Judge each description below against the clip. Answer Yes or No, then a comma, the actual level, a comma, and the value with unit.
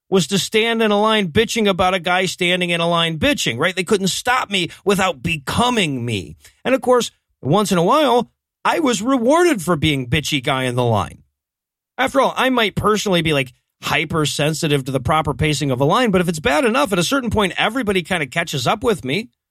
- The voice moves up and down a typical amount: No, wide, 6.6 semitones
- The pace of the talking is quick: Yes, fast, 220 wpm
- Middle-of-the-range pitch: Yes, medium, 180 Hz